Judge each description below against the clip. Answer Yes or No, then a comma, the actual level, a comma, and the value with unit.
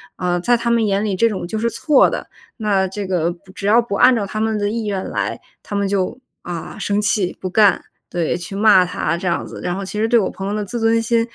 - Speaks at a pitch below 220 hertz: Yes, high, 205 Hz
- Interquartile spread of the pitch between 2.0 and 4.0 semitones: Yes, average, 3.0 semitones